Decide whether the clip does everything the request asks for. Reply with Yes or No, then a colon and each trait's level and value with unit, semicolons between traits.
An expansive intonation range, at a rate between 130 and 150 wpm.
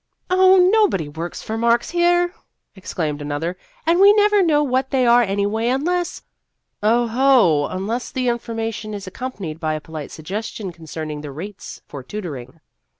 No: wide, 8.7 semitones; average, 170 wpm